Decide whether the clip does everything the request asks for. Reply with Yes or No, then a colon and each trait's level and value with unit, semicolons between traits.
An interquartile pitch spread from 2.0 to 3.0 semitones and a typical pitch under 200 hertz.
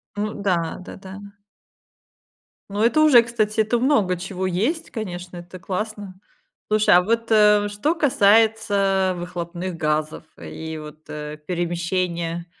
No: average, 3.8 semitones; high, 190 Hz